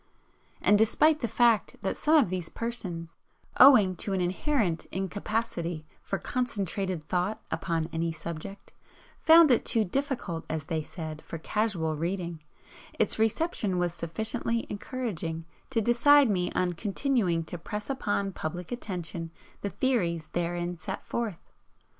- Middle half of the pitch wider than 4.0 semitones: Yes, wide, 5.4 semitones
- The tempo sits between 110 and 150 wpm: Yes, slow, 135 wpm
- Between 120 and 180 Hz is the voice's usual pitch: No, high, 190 Hz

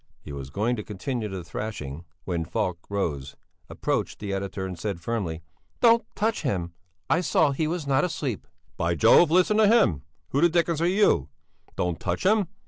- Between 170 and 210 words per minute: Yes, average, 185 wpm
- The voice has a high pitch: No, low, 105 Hz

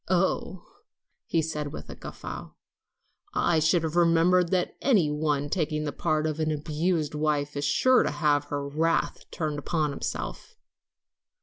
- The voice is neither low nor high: Yes, medium, 155 Hz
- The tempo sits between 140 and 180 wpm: Yes, average, 160 wpm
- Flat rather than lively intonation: Yes, narrow, 2.3 semitones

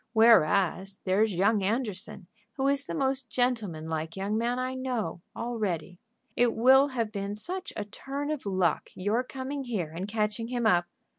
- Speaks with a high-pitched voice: Yes, high, 220 Hz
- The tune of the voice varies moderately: Yes, average, 4.8 semitones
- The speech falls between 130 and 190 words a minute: Yes, average, 170 wpm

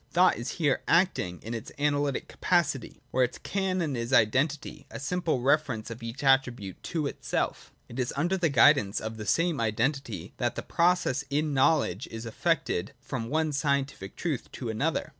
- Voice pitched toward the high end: No, low, 135 Hz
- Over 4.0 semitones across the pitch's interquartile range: Yes, average, 5.2 semitones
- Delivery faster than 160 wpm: Yes, average, 170 wpm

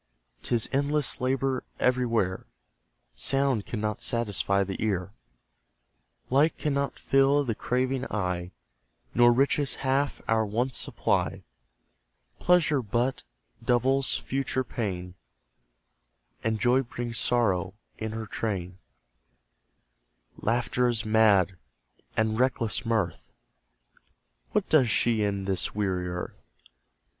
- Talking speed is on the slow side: Yes, slow, 100 wpm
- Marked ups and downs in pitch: No, average, 4.4 semitones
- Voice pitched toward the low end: Yes, low, 115 Hz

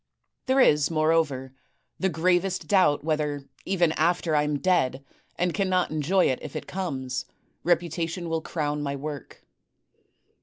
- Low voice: No, medium, 160 Hz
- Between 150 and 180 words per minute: No, average, 140 wpm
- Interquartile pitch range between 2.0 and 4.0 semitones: Yes, average, 3.4 semitones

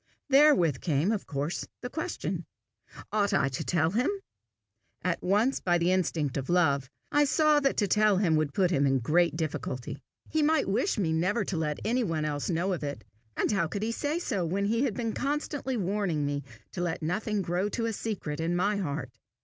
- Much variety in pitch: Yes, wide, 6.0 semitones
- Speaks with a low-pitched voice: No, medium, 185 Hz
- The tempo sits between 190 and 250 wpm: Yes, fast, 205 wpm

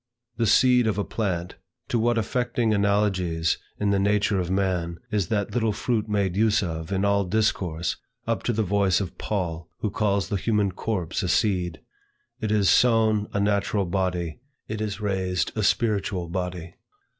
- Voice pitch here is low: Yes, low, 100 Hz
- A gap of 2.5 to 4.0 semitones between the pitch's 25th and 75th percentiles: Yes, average, 2.9 semitones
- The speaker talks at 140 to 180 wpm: Yes, average, 170 wpm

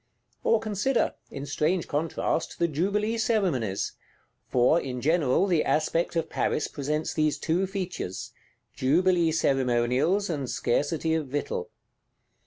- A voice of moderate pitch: Yes, medium, 160 Hz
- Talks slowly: Yes, slow, 120 wpm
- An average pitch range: Yes, average, 4.9 semitones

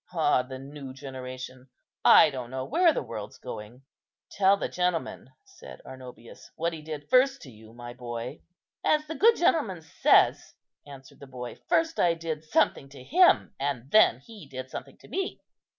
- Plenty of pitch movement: Yes, wide, 6.7 semitones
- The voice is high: No, medium, 140 Hz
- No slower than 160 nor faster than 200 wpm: Yes, average, 170 wpm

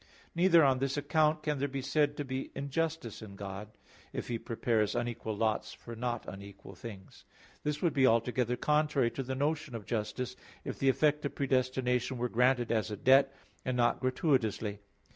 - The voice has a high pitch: No, low, 130 Hz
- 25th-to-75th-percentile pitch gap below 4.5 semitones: Yes, average, 3.6 semitones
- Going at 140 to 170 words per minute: No, average, 180 wpm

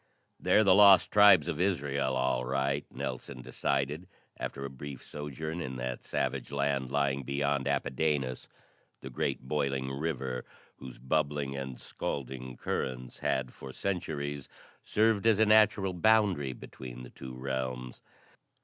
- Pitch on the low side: Yes, very low, 70 Hz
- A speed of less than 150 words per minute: Yes, slow, 135 wpm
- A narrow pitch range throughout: No, average, 3.2 semitones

